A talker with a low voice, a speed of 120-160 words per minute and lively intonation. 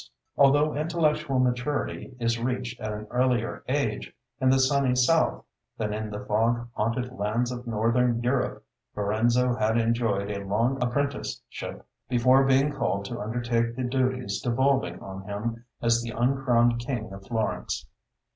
No: low, 120 Hz; average, 145 wpm; average, 2.7 semitones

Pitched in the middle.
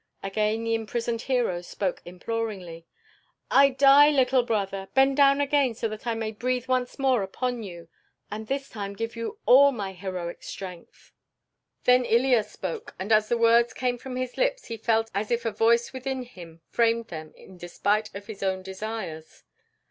No: high, 225 Hz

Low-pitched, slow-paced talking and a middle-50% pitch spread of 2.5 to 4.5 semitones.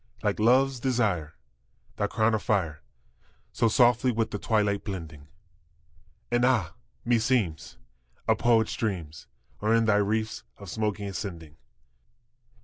Yes: low, 110 Hz; slow, 125 wpm; average, 4.2 semitones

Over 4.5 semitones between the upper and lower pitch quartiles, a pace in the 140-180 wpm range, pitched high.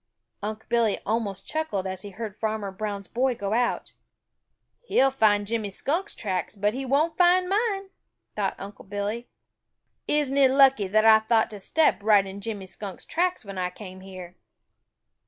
Yes: average, 5.2 semitones; average, 165 wpm; high, 220 Hz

